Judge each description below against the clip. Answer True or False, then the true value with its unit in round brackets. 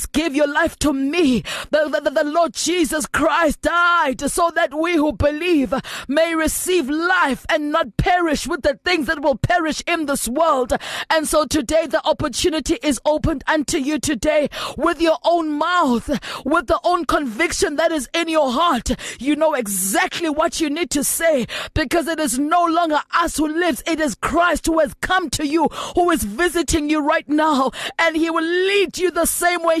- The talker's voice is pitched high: True (315 Hz)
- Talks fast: False (185 wpm)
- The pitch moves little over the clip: True (2.2 semitones)